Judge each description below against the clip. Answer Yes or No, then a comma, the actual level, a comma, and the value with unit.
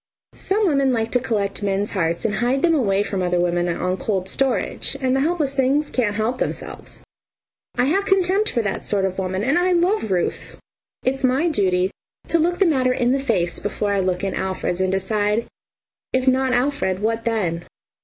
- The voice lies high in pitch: Yes, high, 230 Hz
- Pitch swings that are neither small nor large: No, wide, 6.2 semitones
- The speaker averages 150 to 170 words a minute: No, average, 195 wpm